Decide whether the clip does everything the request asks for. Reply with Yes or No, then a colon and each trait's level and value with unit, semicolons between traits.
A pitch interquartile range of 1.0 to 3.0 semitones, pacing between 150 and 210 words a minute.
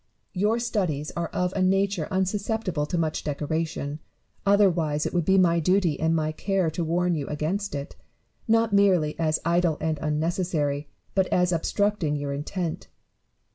No: average, 3.8 semitones; average, 155 wpm